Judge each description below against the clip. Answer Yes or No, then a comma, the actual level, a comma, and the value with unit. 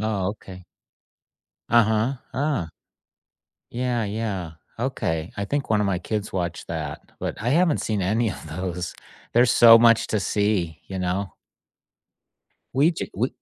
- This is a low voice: Yes, low, 105 Hz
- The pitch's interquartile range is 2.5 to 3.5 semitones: No, average, 4.3 semitones